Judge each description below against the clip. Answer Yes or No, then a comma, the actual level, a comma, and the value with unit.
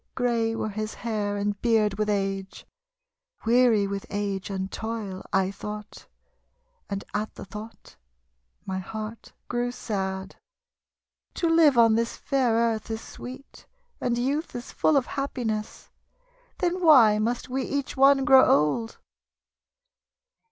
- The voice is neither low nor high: No, high, 225 Hz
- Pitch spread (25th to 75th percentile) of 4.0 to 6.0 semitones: No, average, 3.4 semitones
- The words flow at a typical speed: No, slow, 130 wpm